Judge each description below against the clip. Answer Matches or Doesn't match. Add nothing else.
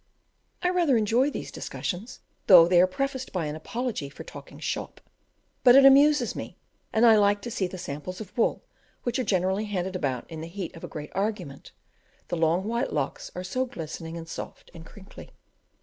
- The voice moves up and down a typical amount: Doesn't match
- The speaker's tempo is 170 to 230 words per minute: Matches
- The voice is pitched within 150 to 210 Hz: Matches